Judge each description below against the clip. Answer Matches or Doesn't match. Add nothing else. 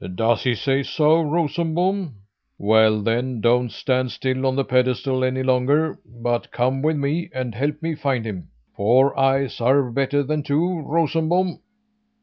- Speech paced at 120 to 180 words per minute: Matches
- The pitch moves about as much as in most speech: Matches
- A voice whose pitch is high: Doesn't match